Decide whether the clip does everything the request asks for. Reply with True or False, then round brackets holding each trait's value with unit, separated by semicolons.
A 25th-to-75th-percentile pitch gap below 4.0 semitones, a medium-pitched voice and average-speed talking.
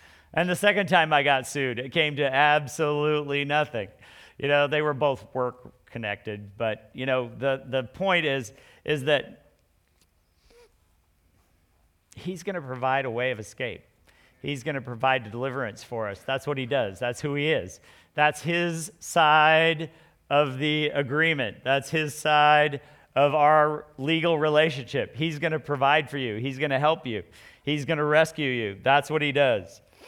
True (3.1 semitones; 145 Hz; 160 wpm)